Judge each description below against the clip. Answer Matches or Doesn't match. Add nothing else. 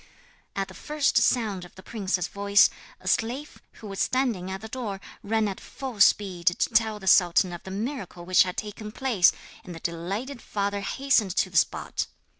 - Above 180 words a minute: Matches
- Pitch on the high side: Matches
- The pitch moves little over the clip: Doesn't match